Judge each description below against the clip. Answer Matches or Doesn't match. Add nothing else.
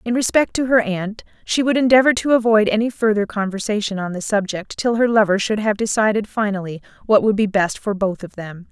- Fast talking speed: Matches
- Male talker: Doesn't match